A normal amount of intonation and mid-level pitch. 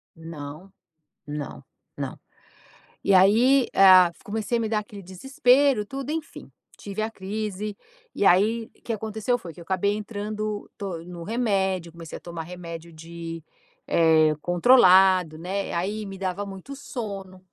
No: average, 3.9 semitones; high, 195 Hz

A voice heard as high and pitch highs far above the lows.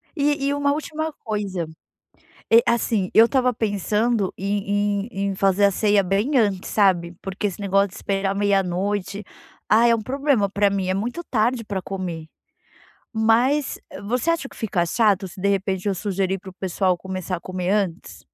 No: high, 200 Hz; average, 3.1 semitones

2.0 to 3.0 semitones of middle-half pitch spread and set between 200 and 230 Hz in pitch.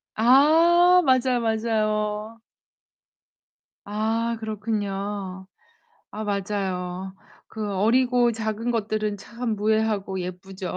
Yes: narrow, 2.6 semitones; high, 215 Hz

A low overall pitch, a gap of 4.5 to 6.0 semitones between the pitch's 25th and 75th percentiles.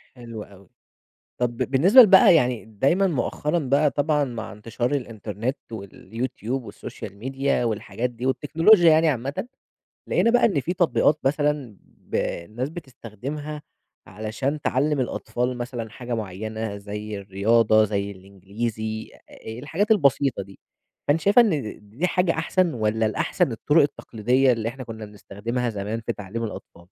Yes: low, 120 Hz; average, 5.1 semitones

